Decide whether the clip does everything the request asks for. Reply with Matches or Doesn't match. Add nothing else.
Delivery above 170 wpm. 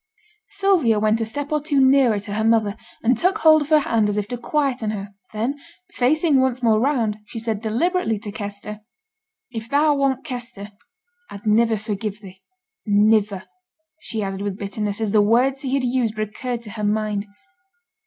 Matches